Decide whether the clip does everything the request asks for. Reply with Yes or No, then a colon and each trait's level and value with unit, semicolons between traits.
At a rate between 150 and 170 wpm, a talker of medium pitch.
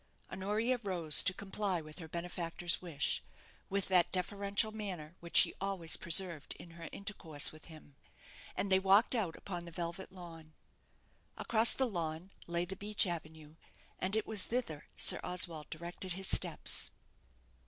Yes: average, 155 wpm; medium, 180 Hz